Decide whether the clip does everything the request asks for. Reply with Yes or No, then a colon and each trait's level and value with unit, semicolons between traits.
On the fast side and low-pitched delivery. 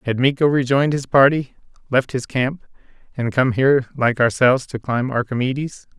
No: average, 160 wpm; low, 130 Hz